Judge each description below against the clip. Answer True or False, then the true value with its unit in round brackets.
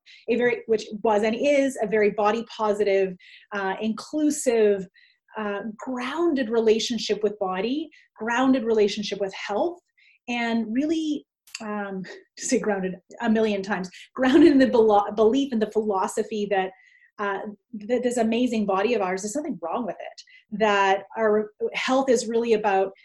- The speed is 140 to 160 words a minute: True (145 wpm)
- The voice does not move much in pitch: False (3.9 semitones)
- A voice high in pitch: True (220 Hz)